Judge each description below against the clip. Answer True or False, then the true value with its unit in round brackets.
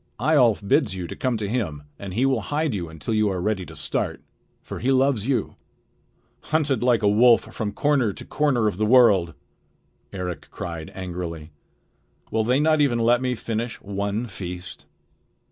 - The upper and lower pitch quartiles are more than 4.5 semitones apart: True (5.2 semitones)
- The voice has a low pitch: True (110 Hz)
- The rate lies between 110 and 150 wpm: False (170 wpm)